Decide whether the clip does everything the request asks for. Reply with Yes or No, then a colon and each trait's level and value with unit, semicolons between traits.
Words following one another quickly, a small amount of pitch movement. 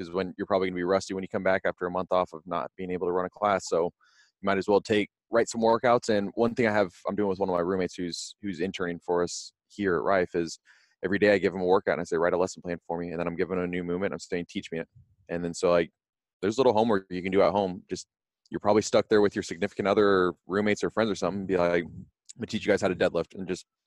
Yes: fast, 305 wpm; narrow, 2.2 semitones